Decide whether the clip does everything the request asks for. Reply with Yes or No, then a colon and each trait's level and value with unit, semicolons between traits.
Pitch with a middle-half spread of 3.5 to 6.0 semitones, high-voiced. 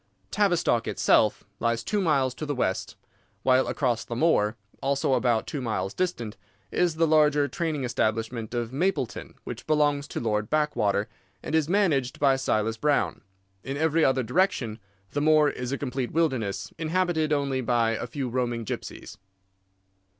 No: average, 4.7 semitones; low, 135 Hz